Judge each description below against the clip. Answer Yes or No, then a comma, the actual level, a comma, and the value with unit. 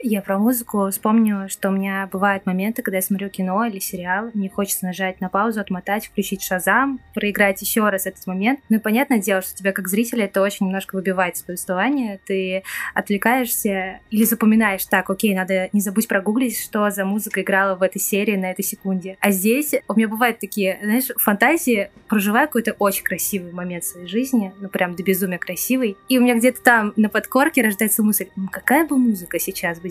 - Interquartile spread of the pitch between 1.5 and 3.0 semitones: Yes, average, 2.7 semitones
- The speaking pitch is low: No, high, 200 Hz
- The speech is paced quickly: Yes, fast, 195 wpm